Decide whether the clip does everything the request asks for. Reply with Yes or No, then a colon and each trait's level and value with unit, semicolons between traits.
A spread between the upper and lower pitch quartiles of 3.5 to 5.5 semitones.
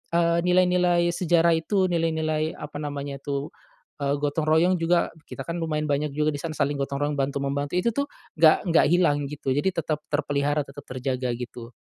No: average, 2.9 semitones